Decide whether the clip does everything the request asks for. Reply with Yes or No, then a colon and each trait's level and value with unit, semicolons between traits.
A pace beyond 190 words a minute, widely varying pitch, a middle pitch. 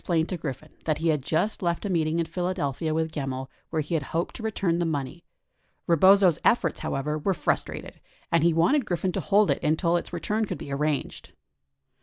No: fast, 205 wpm; average, 2.9 semitones; medium, 165 Hz